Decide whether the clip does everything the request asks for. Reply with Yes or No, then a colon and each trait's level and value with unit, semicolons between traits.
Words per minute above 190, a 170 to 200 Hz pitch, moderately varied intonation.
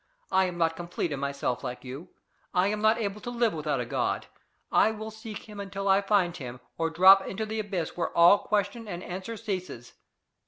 Yes: fast, 205 wpm; high, 190 Hz; average, 4.3 semitones